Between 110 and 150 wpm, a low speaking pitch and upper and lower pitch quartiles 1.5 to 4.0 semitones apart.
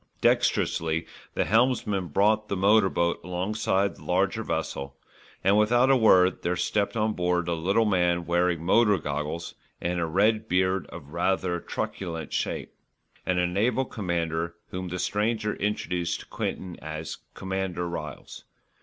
Yes: average, 145 wpm; very low, 90 Hz; average, 3.4 semitones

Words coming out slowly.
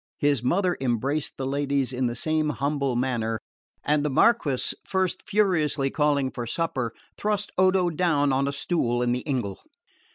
No: average, 160 wpm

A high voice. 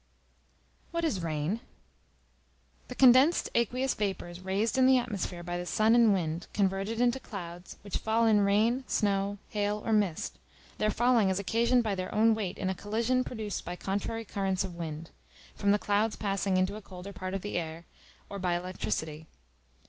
Yes: high, 200 Hz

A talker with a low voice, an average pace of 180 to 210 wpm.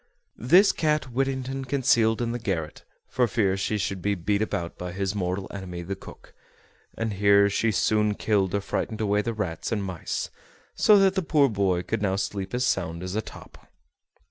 Yes: low, 105 Hz; average, 190 wpm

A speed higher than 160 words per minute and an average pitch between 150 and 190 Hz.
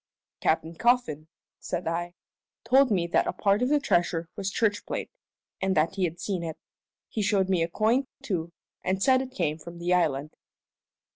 Yes: average, 185 wpm; medium, 185 Hz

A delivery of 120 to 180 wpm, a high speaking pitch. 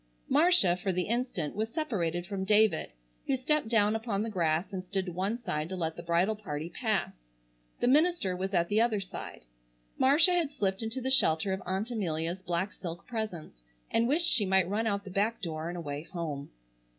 No: average, 200 wpm; high, 195 Hz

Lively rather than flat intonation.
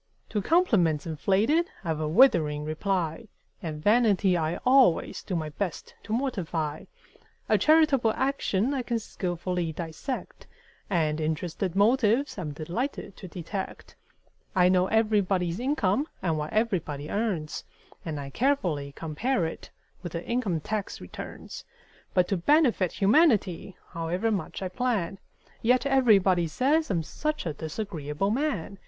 Yes: wide, 6.3 semitones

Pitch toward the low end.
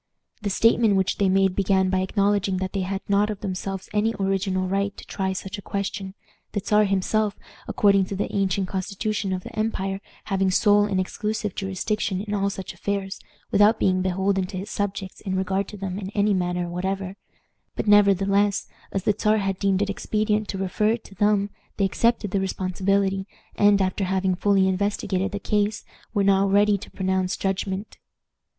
No: high, 195 Hz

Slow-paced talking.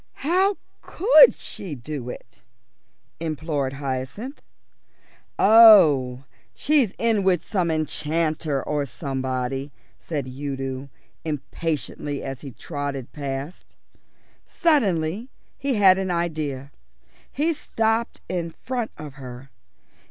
Yes: slow, 100 wpm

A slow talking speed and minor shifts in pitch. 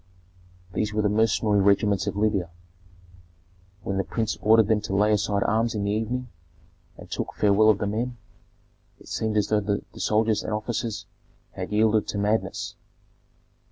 No: average, 160 wpm; narrow, 1.4 semitones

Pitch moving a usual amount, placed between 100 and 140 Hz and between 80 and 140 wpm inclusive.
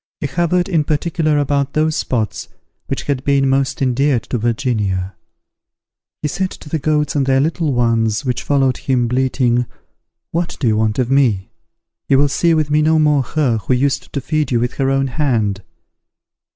No: average, 3.7 semitones; low, 135 Hz; average, 180 wpm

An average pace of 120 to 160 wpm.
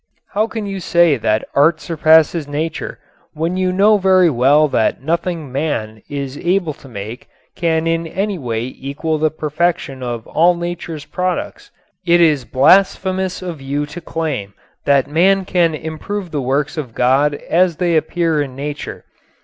Yes: average, 155 wpm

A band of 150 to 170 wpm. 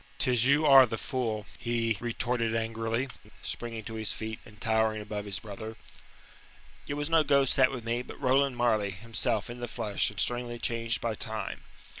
No: average, 180 wpm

